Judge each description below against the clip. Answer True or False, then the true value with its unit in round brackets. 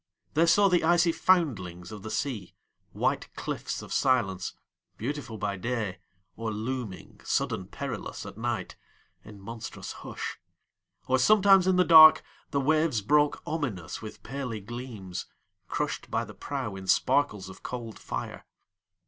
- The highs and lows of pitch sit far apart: True (6.7 semitones)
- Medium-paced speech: False (125 wpm)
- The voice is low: True (120 Hz)